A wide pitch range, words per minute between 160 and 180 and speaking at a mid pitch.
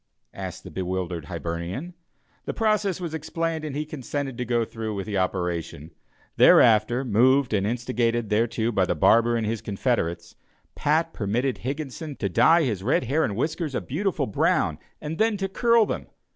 No: wide, 7.2 semitones; average, 170 wpm; low, 120 Hz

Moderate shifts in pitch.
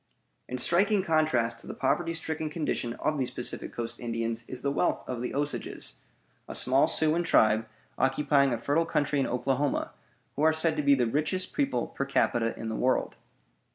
Yes: average, 4.4 semitones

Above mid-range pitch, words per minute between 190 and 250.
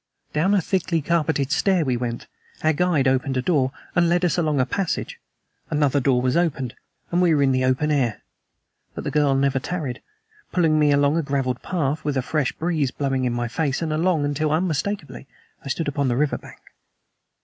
No: medium, 145 Hz; average, 200 wpm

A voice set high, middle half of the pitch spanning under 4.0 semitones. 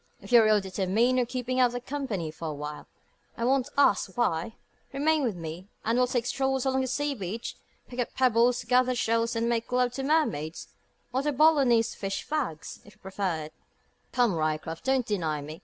No: high, 235 Hz; wide, 5.4 semitones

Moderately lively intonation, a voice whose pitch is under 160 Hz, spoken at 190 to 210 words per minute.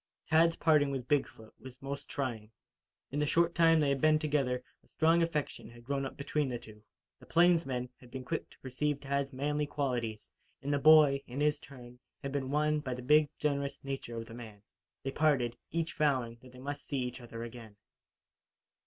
Yes: average, 3.2 semitones; medium, 140 Hz; average, 200 wpm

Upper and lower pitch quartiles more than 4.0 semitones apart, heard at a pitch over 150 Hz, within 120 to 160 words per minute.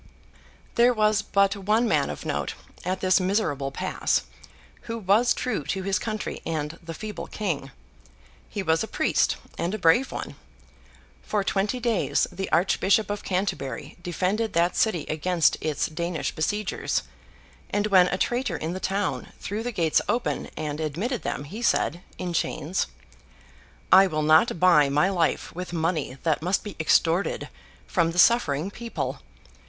Yes: average, 4.5 semitones; medium, 185 Hz; average, 155 wpm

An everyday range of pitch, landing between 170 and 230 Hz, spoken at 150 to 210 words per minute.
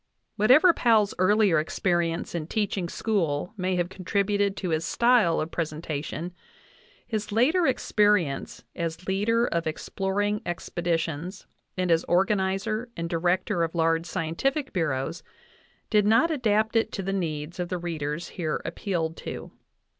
No: average, 4.1 semitones; medium, 185 Hz; average, 140 wpm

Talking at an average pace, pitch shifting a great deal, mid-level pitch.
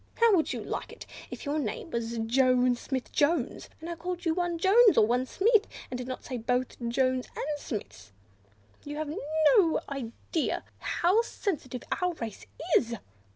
No: average, 180 wpm; wide, 5.7 semitones; very high, 280 Hz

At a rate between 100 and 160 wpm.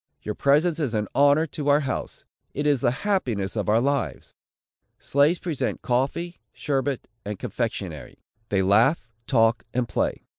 Yes: average, 150 wpm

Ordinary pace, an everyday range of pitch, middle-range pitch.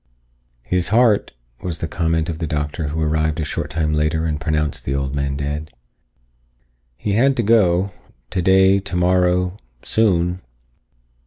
No: average, 145 wpm; average, 3.5 semitones; very low, 85 Hz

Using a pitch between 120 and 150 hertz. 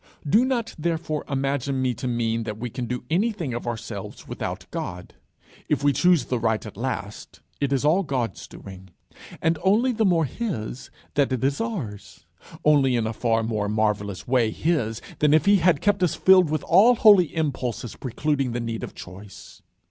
Yes: low, 135 Hz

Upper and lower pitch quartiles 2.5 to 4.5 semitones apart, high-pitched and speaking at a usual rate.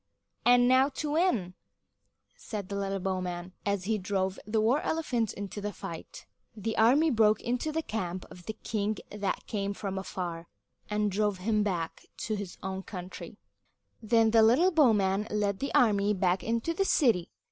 Yes: average, 3.4 semitones; high, 210 Hz; average, 170 wpm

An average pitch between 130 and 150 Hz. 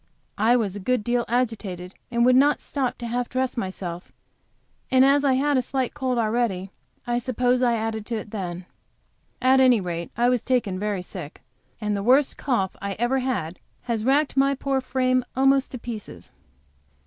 No: high, 240 Hz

